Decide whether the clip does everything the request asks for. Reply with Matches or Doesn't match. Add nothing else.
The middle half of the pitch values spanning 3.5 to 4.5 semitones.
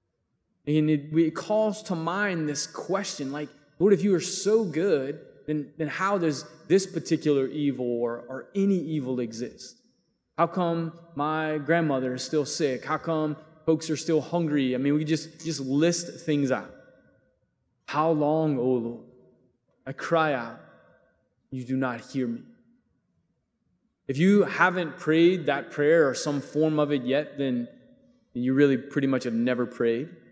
Matches